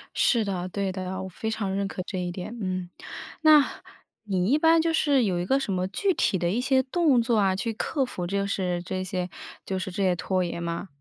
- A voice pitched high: Yes, high, 195 Hz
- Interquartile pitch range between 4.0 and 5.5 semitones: Yes, average, 4.8 semitones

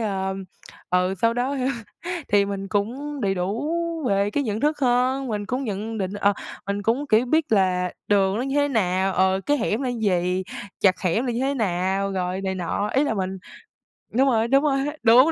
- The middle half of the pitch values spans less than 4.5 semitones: No, average, 4.9 semitones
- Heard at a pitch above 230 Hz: No, high, 210 Hz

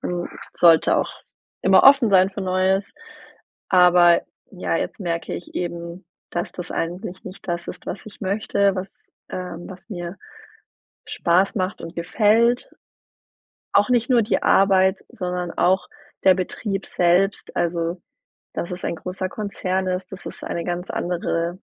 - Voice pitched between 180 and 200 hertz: Yes, medium, 185 Hz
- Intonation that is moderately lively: No, narrow, 2.1 semitones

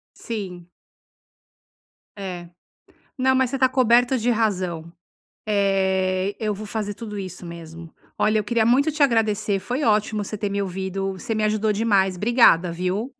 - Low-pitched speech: No, high, 205 Hz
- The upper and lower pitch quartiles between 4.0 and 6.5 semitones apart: No, average, 3.4 semitones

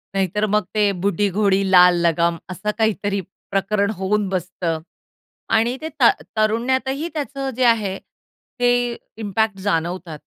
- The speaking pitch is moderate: No, high, 205 Hz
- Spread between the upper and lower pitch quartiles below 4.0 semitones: Yes, average, 3.4 semitones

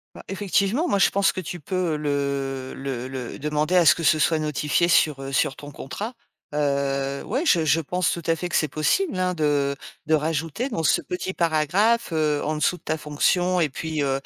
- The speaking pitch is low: No, medium, 155 Hz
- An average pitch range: Yes, average, 3.9 semitones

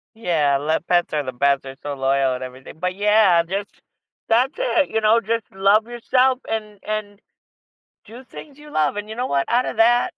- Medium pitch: No, high, 205 Hz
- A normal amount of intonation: No, wide, 7.7 semitones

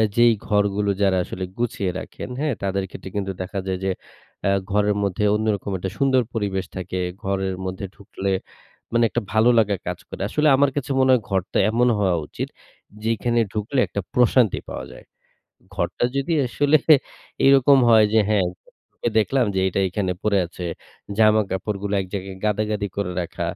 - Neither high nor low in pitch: No, low, 105 Hz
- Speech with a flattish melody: No, average, 3.5 semitones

